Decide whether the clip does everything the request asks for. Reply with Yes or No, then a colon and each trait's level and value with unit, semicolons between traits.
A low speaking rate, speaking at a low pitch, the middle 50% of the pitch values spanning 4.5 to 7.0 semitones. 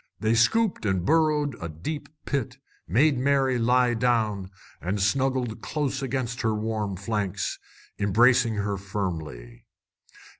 Yes: slow, 120 wpm; low, 115 Hz; average, 4.8 semitones